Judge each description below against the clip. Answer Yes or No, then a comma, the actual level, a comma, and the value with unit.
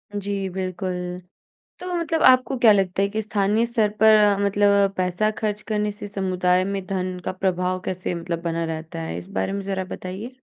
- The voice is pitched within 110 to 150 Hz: No, high, 195 Hz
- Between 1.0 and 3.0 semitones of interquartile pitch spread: Yes, narrow, 2.6 semitones